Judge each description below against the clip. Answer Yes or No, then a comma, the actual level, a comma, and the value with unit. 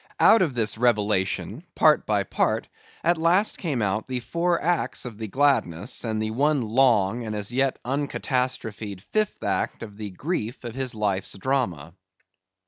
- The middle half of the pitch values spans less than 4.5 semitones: No, average, 4.9 semitones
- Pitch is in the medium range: No, low, 120 Hz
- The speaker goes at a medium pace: Yes, average, 160 wpm